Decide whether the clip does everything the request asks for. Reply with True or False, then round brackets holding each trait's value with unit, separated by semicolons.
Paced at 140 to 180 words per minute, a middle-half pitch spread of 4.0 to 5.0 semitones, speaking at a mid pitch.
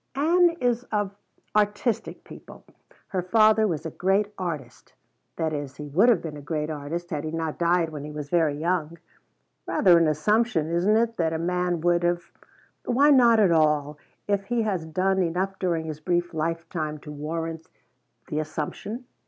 True (175 wpm; 4.6 semitones; 170 Hz)